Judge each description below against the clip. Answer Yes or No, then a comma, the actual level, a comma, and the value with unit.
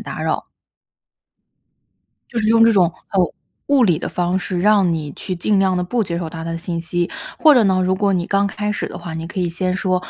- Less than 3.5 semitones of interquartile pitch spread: Yes, average, 3.1 semitones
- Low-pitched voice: No, medium, 185 Hz